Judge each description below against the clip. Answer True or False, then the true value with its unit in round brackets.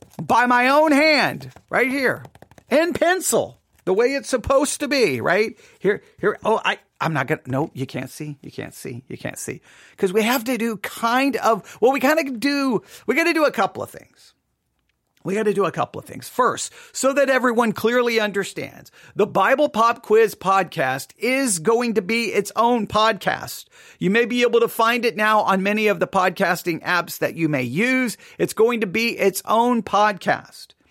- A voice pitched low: False (225 Hz)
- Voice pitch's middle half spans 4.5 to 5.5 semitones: True (5.0 semitones)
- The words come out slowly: False (200 wpm)